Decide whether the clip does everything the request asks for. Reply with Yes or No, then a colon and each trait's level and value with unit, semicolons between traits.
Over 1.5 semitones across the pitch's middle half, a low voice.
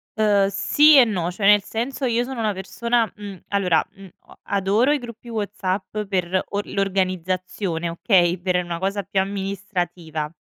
No: narrow, 2.5 semitones; high, 195 Hz